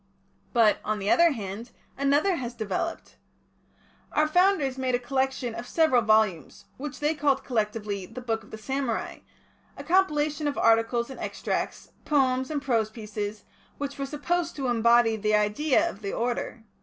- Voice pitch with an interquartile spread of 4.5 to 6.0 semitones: Yes, average, 4.9 semitones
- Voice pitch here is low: No, very high, 250 Hz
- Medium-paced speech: Yes, average, 160 wpm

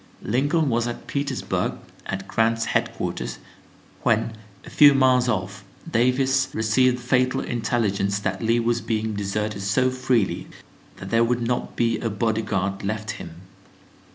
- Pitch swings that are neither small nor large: Yes, average, 3.3 semitones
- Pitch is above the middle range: No, low, 115 Hz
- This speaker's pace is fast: No, average, 145 wpm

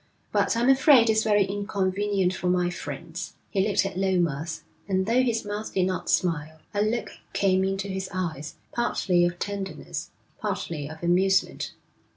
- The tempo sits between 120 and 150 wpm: No, average, 160 wpm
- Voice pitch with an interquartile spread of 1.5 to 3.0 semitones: Yes, average, 2.7 semitones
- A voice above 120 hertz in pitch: Yes, high, 190 Hz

